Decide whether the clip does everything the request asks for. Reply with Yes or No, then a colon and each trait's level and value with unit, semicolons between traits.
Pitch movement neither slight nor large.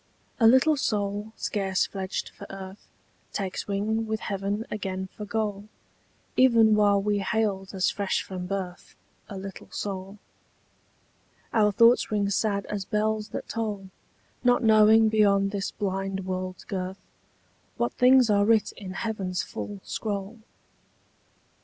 No: narrow, 2.1 semitones